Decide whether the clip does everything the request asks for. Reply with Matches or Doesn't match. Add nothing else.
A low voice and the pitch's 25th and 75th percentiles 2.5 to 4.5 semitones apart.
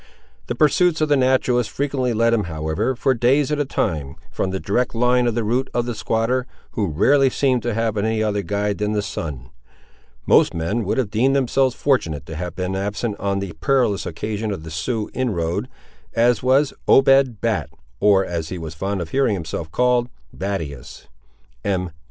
Doesn't match